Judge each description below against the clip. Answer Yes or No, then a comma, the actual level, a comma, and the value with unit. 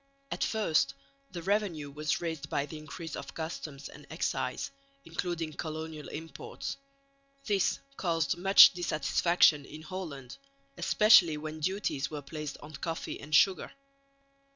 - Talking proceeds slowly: Yes, slow, 130 wpm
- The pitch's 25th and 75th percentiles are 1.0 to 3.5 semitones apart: Yes, average, 2.9 semitones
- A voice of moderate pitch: Yes, medium, 160 Hz